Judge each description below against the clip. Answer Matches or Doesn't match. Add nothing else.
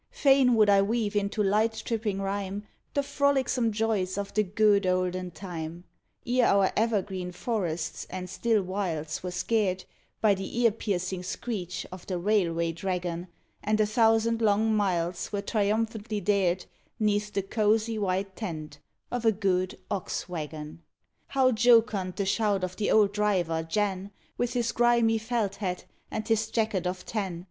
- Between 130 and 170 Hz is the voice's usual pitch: Doesn't match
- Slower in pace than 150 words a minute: Doesn't match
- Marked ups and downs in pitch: Doesn't match